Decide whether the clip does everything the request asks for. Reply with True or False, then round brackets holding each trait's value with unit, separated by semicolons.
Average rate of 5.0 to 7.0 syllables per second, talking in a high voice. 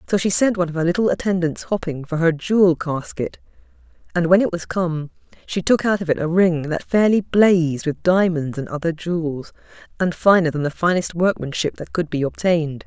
False (5.5 syllables/s; 170 Hz)